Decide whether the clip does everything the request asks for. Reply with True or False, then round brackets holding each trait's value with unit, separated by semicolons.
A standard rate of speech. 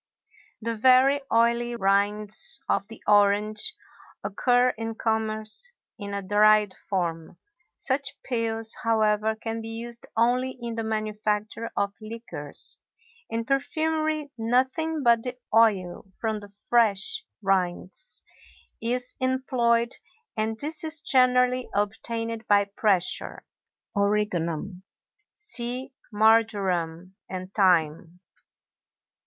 False (100 wpm)